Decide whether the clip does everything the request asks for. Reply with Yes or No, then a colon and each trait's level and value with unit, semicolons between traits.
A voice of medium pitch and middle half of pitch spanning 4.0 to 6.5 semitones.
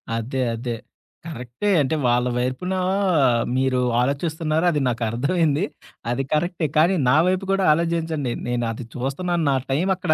Yes: medium, 145 Hz; average, 5.2 semitones